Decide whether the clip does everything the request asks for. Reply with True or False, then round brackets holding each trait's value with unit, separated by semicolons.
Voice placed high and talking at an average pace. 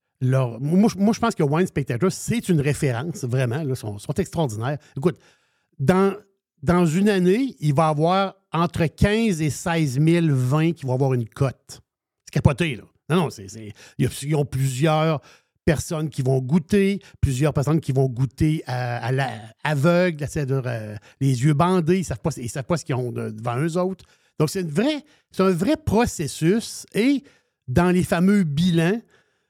False (155 Hz; 180 wpm)